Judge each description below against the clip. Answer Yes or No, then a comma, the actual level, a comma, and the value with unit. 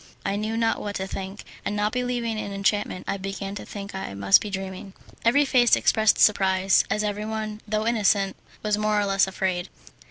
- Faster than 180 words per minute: Yes, average, 190 wpm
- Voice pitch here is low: No, high, 205 Hz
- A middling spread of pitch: No, narrow, 1.9 semitones